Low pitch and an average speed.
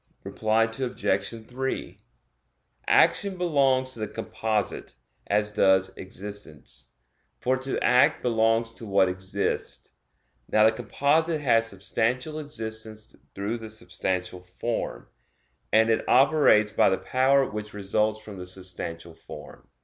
No: low, 110 Hz; slow, 120 wpm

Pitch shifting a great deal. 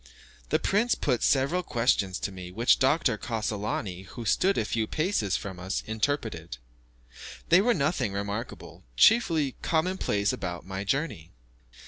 Yes: wide, 7.9 semitones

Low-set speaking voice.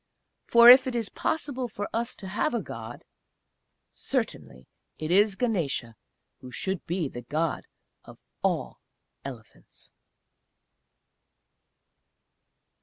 No: high, 190 Hz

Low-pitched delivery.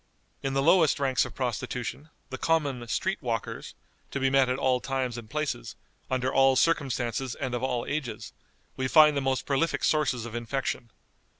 Yes: low, 130 Hz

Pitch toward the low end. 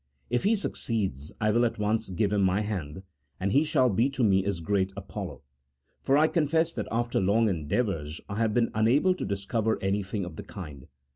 Yes: low, 105 Hz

